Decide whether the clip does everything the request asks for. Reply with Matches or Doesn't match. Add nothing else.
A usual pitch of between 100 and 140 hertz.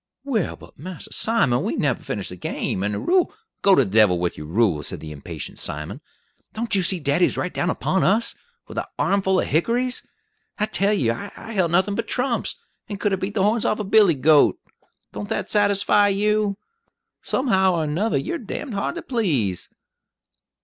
Doesn't match